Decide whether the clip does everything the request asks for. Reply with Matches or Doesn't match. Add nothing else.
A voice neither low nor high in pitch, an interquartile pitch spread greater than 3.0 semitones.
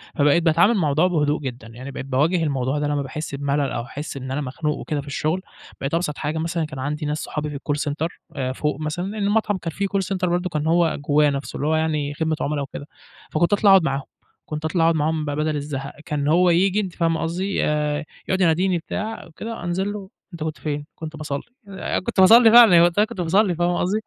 Matches